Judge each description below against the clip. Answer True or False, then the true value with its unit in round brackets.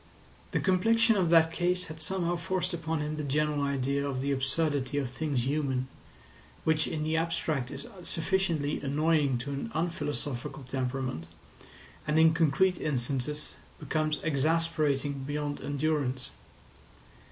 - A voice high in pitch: False (150 Hz)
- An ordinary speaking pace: False (130 wpm)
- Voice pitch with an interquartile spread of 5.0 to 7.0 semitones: False (3.0 semitones)